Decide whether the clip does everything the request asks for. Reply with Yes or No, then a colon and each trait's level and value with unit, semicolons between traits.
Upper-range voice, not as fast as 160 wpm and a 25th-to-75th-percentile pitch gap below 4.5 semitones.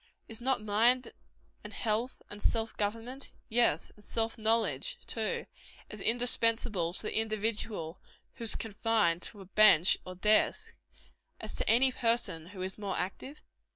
Yes: high, 220 Hz; average, 150 wpm; narrow, 2.5 semitones